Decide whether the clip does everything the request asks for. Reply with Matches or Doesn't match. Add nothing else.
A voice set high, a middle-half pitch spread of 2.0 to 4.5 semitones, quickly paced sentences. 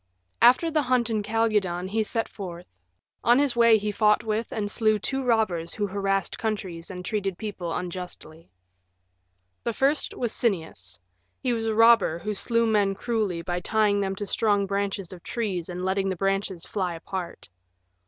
Doesn't match